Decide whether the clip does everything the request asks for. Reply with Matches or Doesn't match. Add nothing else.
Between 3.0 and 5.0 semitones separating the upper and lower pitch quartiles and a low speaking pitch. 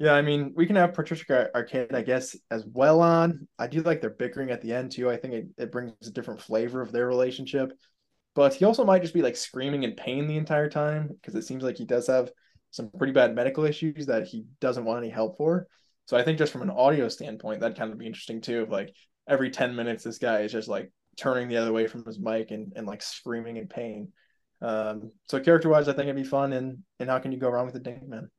Matches